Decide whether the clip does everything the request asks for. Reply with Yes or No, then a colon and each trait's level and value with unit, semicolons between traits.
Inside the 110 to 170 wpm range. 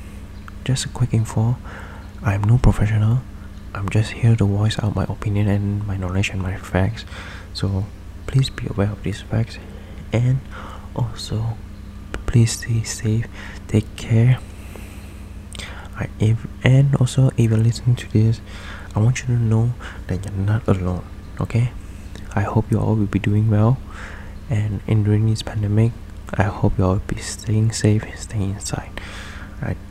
Yes: average, 160 wpm